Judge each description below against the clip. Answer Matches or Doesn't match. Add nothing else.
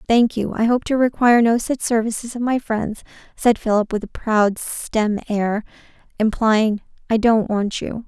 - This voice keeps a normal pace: Matches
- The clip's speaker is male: Doesn't match